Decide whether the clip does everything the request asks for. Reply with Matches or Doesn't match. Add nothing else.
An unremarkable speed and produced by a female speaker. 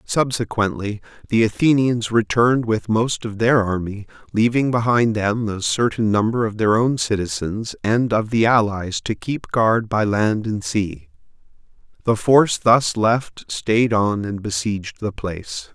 Doesn't match